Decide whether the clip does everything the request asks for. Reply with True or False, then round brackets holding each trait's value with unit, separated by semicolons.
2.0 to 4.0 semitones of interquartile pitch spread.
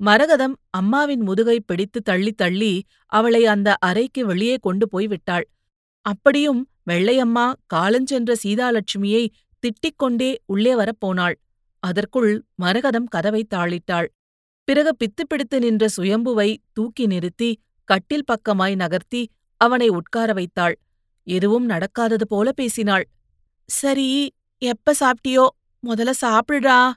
False (4.5 semitones)